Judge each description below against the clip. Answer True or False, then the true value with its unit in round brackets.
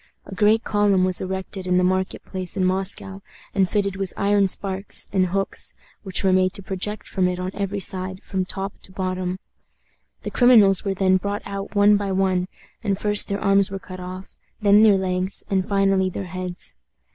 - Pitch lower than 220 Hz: True (190 Hz)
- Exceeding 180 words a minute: True (190 wpm)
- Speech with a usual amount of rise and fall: False (1.3 semitones)